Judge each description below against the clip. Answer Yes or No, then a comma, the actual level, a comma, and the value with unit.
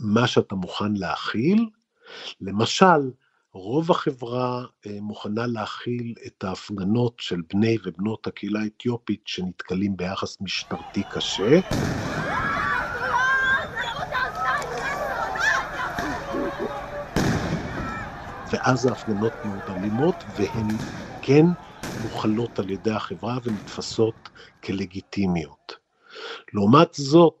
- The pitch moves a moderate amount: Yes, average, 4.3 semitones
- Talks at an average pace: No, slow, 70 wpm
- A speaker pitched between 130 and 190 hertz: No, low, 115 Hz